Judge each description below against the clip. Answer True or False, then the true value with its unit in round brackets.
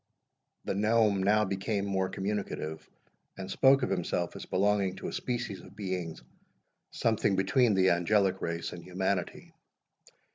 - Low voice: True (95 Hz)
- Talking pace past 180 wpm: False (140 wpm)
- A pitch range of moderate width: False (2.2 semitones)